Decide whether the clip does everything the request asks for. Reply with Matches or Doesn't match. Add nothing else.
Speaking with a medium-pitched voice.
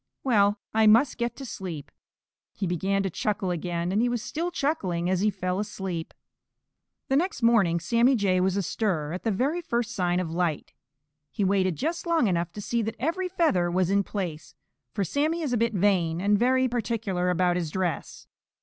Doesn't match